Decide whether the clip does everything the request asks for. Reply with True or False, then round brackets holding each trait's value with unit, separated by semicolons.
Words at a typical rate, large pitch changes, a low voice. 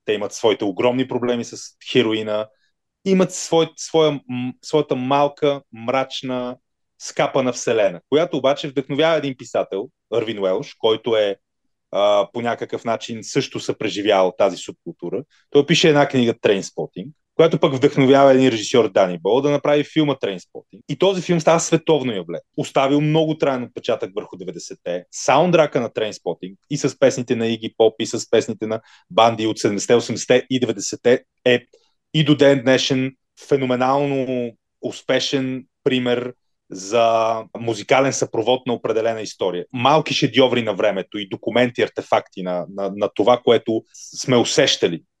False (140 wpm; 4.1 semitones; 130 Hz)